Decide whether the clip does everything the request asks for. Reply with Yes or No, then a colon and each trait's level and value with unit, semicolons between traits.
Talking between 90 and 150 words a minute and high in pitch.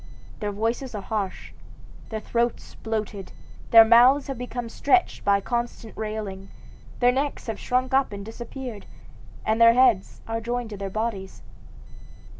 Yes: average, 145 wpm; high, 225 Hz